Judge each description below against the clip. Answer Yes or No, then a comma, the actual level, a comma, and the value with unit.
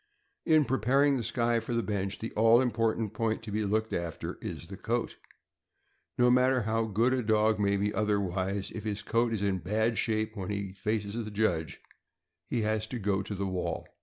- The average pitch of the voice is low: Yes, low, 110 Hz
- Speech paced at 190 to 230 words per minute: Yes, average, 195 wpm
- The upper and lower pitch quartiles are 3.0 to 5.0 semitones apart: No, narrow, 2.4 semitones